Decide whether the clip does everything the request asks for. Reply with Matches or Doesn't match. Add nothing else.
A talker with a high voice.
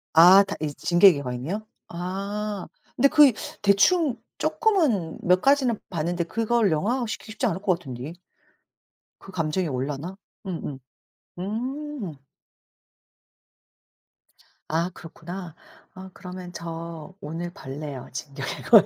Doesn't match